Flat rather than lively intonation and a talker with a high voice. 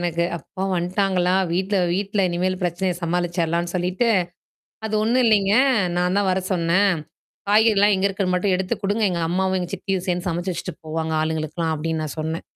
No: narrow, 2.3 semitones; medium, 180 Hz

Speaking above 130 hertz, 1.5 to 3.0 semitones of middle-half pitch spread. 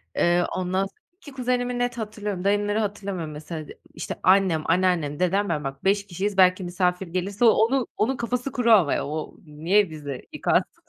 No: high, 190 Hz; average, 3.8 semitones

